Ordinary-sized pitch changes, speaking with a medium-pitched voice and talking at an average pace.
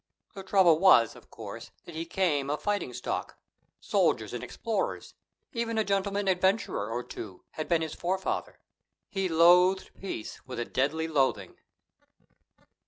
Yes: average, 4.5 semitones; medium, 175 Hz; average, 145 wpm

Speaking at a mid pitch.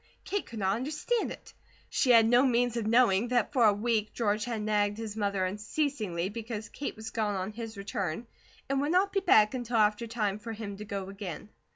No: high, 220 Hz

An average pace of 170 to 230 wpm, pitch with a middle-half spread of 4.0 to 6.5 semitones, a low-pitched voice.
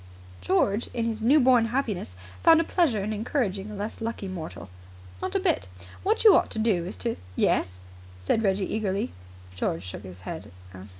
No: average, 185 wpm; average, 4.3 semitones; high, 210 Hz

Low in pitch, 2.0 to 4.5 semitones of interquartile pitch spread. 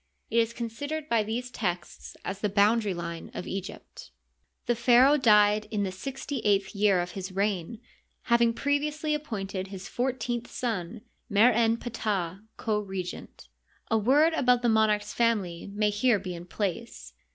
No: high, 215 Hz; average, 3.7 semitones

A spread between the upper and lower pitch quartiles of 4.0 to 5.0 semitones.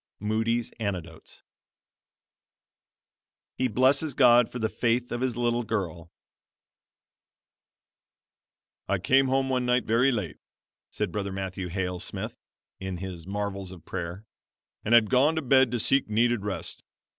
Yes: average, 4.5 semitones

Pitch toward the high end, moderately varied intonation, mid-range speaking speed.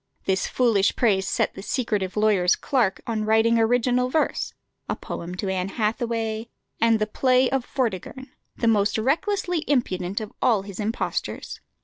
Yes: high, 225 Hz; average, 3.9 semitones; average, 150 wpm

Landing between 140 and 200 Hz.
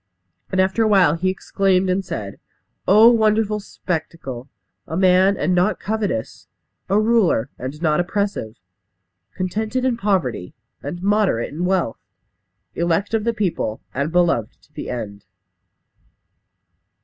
Yes: medium, 185 Hz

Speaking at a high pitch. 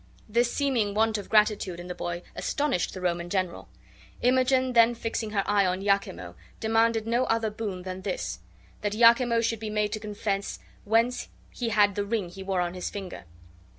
Yes: high, 210 Hz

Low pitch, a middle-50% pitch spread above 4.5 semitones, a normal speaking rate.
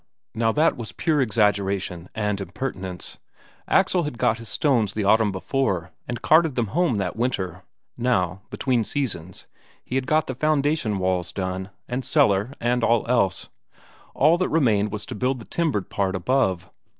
Yes: low, 110 Hz; wide, 5.6 semitones; average, 160 wpm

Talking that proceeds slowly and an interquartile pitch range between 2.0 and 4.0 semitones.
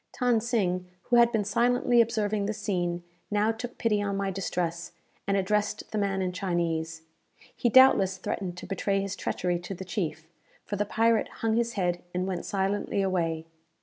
No: average, 180 wpm; average, 3.4 semitones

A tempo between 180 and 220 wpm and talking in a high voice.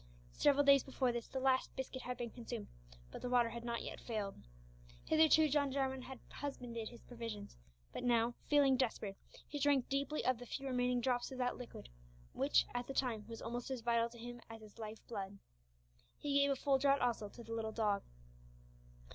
Yes: average, 195 wpm; high, 245 Hz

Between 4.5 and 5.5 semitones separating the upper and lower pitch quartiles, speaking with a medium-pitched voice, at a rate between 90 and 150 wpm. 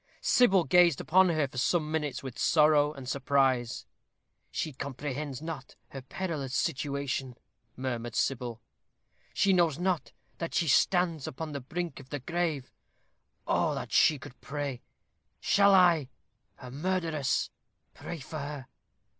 No: average, 4.1 semitones; medium, 145 Hz; average, 140 wpm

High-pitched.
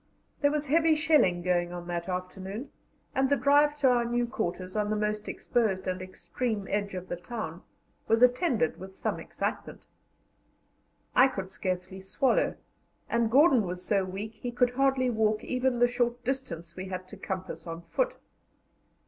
Yes: high, 215 Hz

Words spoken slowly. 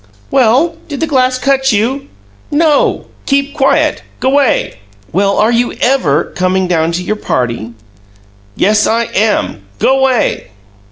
Yes: slow, 125 wpm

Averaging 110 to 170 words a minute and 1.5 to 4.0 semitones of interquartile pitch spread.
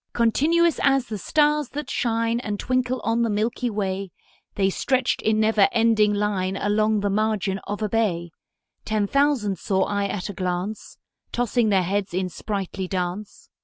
Yes: average, 165 wpm; average, 3.2 semitones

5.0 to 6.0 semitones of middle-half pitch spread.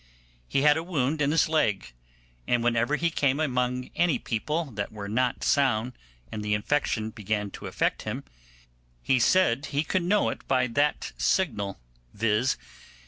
Yes: wide, 5.5 semitones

